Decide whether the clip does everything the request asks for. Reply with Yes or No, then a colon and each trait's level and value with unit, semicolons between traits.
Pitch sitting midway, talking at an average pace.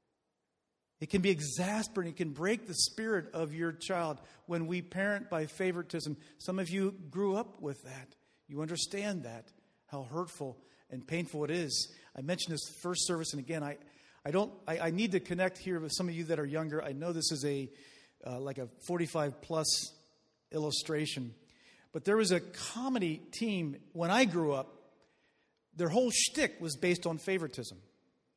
Yes: medium, 165 Hz; average, 180 wpm